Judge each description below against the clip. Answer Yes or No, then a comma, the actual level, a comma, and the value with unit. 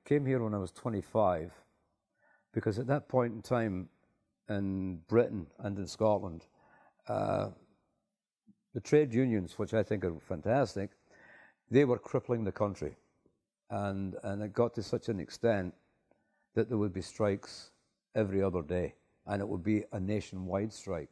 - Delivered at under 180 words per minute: Yes, average, 155 wpm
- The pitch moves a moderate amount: Yes, average, 3.4 semitones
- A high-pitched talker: No, low, 105 Hz